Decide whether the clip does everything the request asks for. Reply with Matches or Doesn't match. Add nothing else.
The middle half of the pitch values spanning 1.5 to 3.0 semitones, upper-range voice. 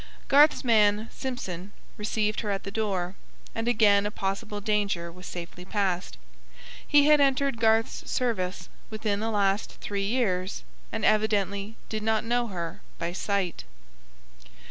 Matches